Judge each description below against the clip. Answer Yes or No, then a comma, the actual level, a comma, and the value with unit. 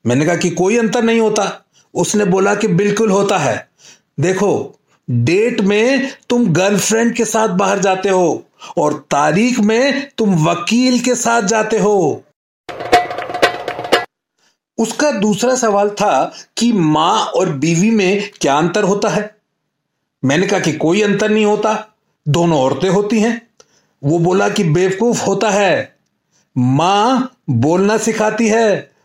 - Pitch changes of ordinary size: Yes, average, 3.5 semitones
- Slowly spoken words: No, average, 135 wpm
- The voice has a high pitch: Yes, high, 205 Hz